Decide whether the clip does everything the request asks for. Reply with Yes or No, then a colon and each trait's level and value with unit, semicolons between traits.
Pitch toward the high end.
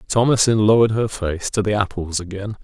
No: low, 105 Hz